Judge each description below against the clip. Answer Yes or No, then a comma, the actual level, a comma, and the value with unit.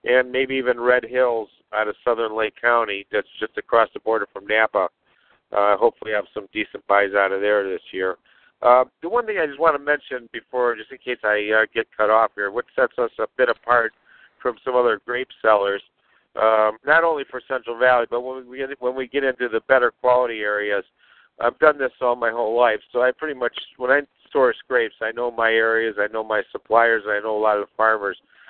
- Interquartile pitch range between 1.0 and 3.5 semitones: Yes, average, 3.1 semitones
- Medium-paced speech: No, fast, 225 wpm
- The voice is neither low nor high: No, low, 120 Hz